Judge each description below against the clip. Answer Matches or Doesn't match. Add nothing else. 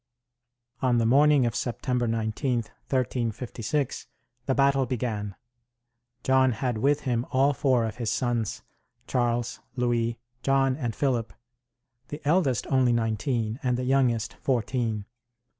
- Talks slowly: Matches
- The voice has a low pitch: Matches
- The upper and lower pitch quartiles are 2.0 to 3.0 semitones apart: Matches